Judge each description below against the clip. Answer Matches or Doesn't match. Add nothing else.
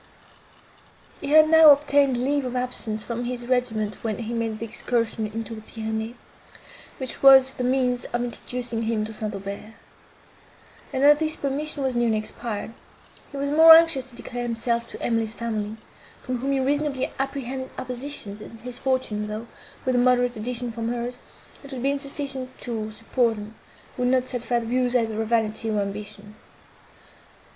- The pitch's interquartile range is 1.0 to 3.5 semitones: Matches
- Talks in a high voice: Matches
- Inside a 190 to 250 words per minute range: Doesn't match